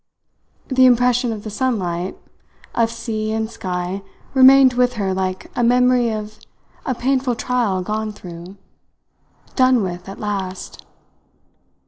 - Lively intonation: No, average, 4.6 semitones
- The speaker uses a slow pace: Yes, slow, 125 wpm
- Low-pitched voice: No, high, 220 Hz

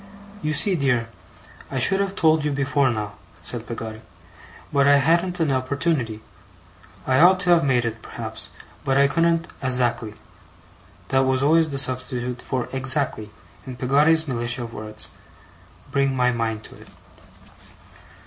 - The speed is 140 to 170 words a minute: Yes, average, 150 wpm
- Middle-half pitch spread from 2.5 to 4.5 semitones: Yes, average, 4.0 semitones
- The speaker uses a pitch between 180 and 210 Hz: No, low, 135 Hz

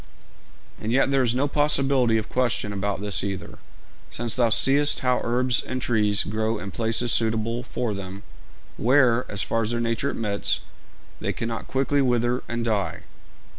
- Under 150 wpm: No, average, 165 wpm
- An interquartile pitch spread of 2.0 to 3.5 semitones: Yes, average, 2.8 semitones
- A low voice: Yes, low, 115 Hz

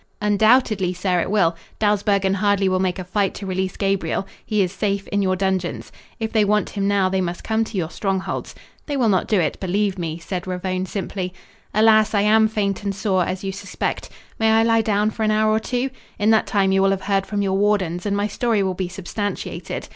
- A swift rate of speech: Yes, fast, 225 wpm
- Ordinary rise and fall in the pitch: No, narrow, 2.1 semitones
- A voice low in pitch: No, high, 200 Hz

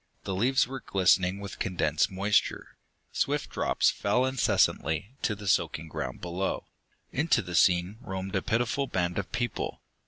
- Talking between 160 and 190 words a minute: No, average, 150 wpm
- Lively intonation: No, average, 4.6 semitones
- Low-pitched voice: Yes, low, 100 Hz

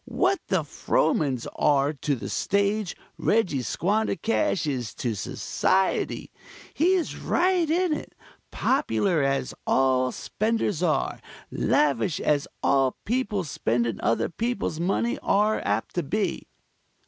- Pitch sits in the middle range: Yes, medium, 180 Hz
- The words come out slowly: Yes, slow, 115 wpm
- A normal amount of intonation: No, wide, 8.3 semitones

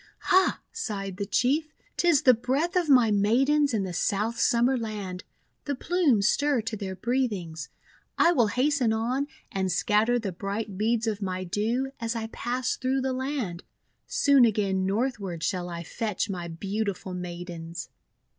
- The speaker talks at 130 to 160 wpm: Yes, average, 155 wpm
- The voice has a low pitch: No, high, 220 Hz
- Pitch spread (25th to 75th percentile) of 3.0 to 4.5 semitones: No, average, 5.2 semitones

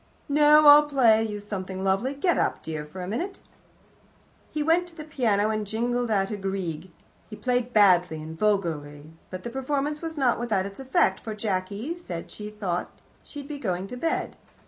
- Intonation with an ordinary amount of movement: No, wide, 6.7 semitones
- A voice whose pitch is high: Yes, high, 215 Hz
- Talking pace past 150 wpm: Yes, average, 190 wpm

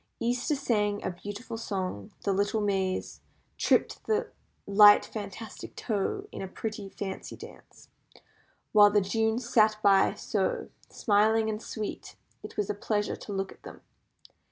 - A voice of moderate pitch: No, high, 210 Hz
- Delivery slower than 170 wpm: Yes, average, 145 wpm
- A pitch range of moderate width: No, narrow, 2.0 semitones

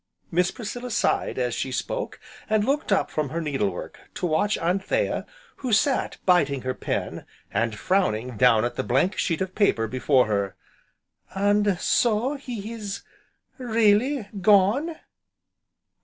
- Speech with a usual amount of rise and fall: No, wide, 8.6 semitones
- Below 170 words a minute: Yes, average, 140 wpm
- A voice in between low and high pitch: No, high, 195 Hz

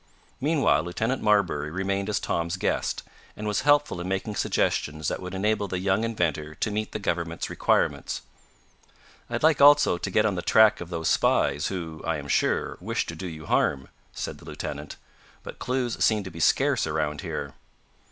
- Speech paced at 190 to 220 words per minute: No, average, 180 wpm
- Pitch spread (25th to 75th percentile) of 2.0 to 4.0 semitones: No, average, 4.9 semitones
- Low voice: Yes, very low, 95 Hz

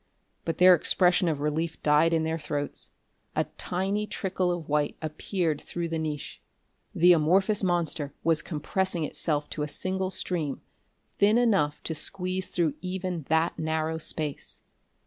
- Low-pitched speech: No, medium, 165 Hz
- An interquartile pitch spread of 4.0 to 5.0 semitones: No, average, 3.1 semitones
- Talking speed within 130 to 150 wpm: Yes, average, 145 wpm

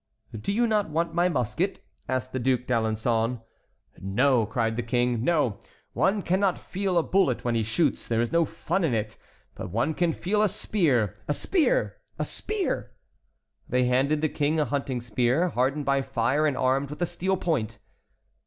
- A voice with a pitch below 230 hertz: Yes, medium, 140 Hz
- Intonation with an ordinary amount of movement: No, wide, 6.4 semitones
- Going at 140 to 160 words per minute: No, average, 180 wpm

